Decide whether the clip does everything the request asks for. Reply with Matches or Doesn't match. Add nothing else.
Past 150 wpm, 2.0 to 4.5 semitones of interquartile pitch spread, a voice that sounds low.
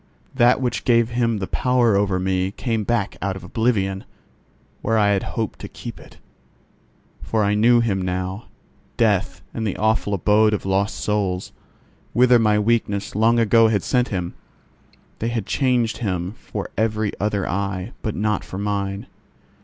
Matches